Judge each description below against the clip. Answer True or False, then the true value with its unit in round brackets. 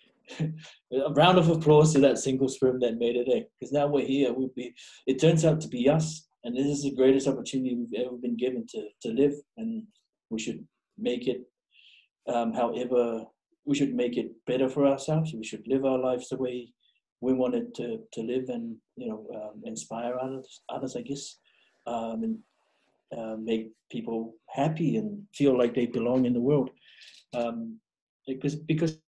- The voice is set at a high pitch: False (130 Hz)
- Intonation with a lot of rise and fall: False (3.4 semitones)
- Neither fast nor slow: True (180 wpm)